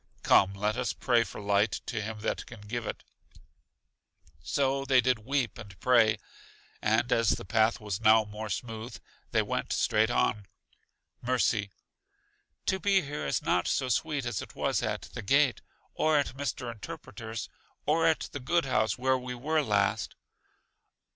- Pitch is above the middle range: No, low, 120 Hz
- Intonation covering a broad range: No, average, 4.1 semitones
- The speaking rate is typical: Yes, average, 160 wpm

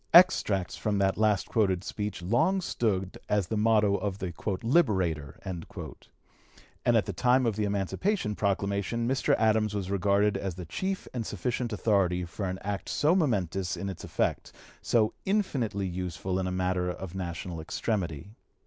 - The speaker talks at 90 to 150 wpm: No, average, 160 wpm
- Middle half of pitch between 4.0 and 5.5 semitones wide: No, average, 3.3 semitones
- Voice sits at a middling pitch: No, low, 100 Hz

